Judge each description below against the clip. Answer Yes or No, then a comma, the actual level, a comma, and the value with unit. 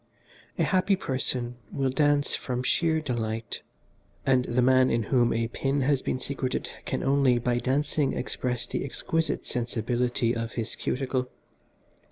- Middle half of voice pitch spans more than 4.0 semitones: No, narrow, 2.4 semitones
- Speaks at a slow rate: No, average, 145 wpm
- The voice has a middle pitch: No, low, 130 Hz